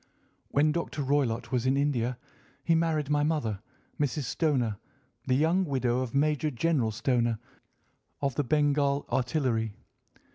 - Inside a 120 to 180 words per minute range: Yes, slow, 135 wpm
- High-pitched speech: No, medium, 140 Hz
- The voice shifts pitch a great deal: No, average, 3.7 semitones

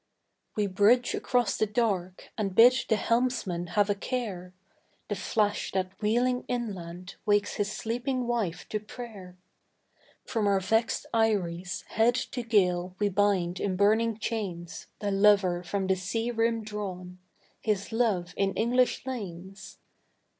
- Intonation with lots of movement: No, average, 3.6 semitones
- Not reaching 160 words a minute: Yes, average, 140 wpm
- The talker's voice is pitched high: Yes, high, 205 Hz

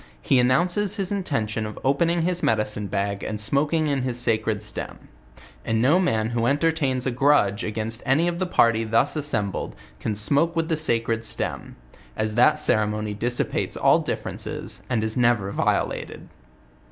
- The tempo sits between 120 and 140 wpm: No, average, 165 wpm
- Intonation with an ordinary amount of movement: No, wide, 5.7 semitones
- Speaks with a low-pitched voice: Yes, low, 120 Hz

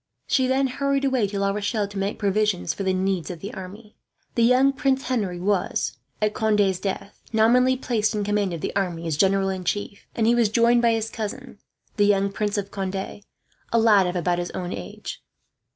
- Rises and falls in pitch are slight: No, average, 3.2 semitones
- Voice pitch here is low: No, high, 205 Hz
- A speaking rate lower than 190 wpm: No, fast, 205 wpm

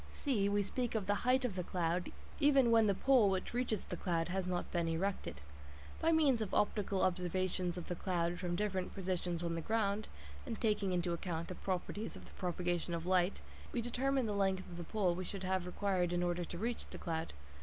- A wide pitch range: No, average, 3.2 semitones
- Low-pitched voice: No, medium, 185 Hz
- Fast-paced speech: Yes, fast, 215 wpm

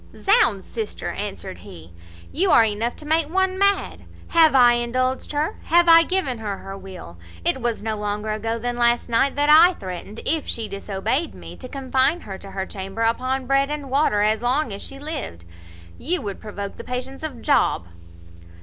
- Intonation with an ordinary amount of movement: No, wide, 6.1 semitones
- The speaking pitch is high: Yes, high, 245 Hz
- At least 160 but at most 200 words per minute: Yes, average, 185 wpm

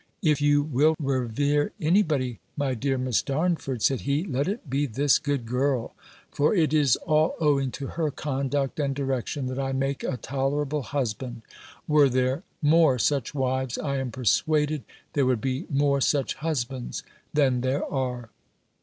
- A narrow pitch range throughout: Yes, narrow, 2.3 semitones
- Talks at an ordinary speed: Yes, average, 165 wpm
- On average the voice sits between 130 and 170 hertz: Yes, medium, 140 Hz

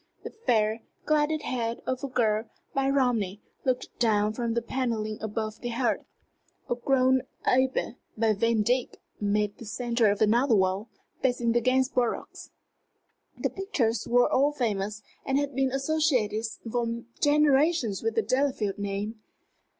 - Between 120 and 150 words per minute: Yes, average, 140 wpm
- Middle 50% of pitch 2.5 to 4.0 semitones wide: Yes, average, 3.4 semitones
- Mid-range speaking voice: No, high, 235 Hz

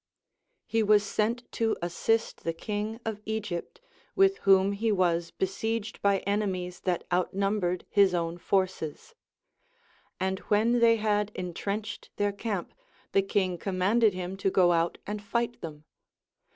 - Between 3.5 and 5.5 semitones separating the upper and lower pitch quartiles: No, average, 3.1 semitones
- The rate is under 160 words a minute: Yes, average, 140 wpm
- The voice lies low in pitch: No, high, 200 Hz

